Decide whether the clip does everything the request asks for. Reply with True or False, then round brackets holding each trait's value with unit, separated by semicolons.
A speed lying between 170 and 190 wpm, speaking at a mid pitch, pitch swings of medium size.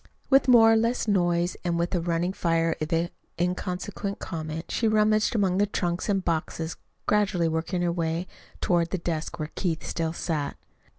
True (175 wpm; 175 Hz; 3.2 semitones)